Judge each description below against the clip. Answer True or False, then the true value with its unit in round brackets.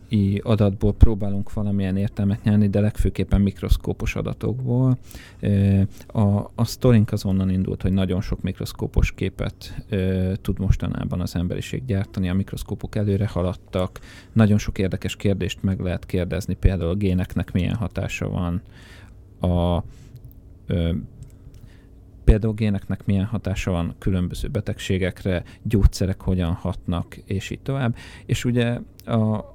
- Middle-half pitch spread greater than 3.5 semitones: False (2.8 semitones)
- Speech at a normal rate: True (120 wpm)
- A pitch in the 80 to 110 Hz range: True (100 Hz)